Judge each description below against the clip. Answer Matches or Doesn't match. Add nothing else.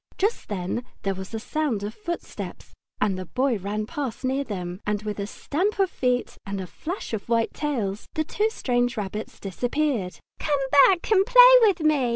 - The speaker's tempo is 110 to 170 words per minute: Doesn't match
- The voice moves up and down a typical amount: Doesn't match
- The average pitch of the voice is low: Doesn't match